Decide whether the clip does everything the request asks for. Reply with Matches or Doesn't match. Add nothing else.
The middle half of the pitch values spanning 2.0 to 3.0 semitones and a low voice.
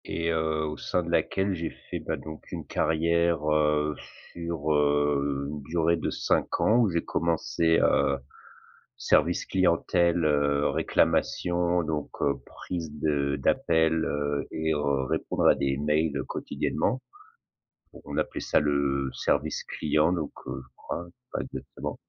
Matches